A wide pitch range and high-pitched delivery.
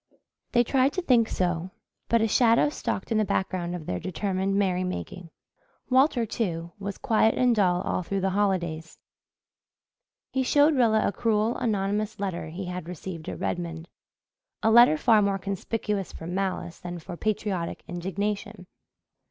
No: average, 3.9 semitones; high, 195 Hz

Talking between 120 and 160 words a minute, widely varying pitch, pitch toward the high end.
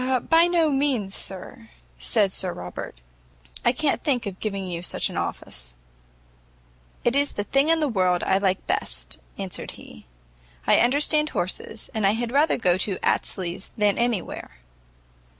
Yes: average, 155 wpm; wide, 7.0 semitones; high, 205 Hz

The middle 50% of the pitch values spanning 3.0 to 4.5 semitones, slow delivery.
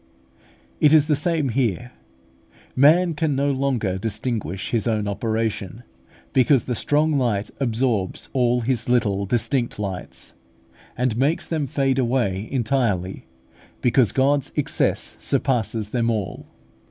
Yes: average, 4.0 semitones; slow, 125 wpm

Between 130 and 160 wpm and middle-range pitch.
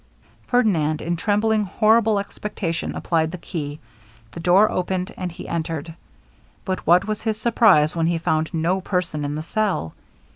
Yes: average, 155 wpm; medium, 180 Hz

